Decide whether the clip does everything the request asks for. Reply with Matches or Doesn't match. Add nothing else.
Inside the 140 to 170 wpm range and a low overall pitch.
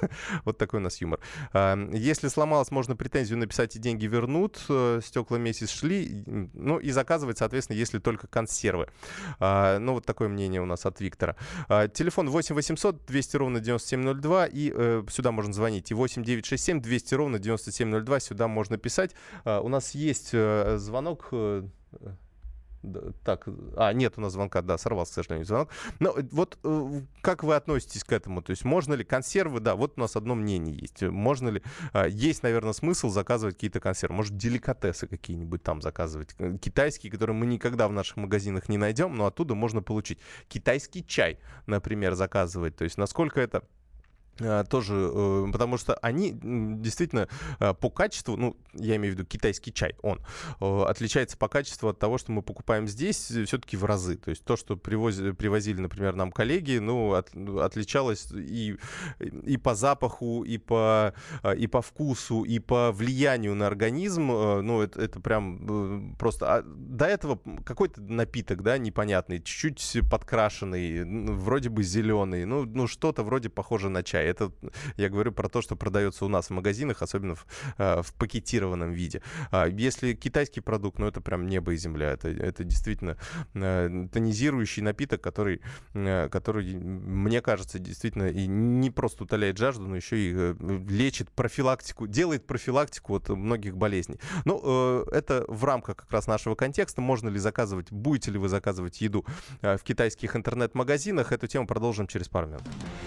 Matches